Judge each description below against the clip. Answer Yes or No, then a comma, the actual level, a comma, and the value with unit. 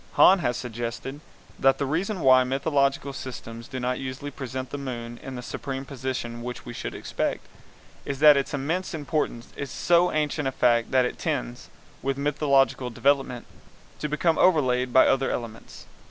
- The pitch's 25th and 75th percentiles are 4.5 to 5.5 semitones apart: No, narrow, 2.6 semitones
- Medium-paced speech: Yes, average, 170 wpm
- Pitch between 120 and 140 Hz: Yes, low, 135 Hz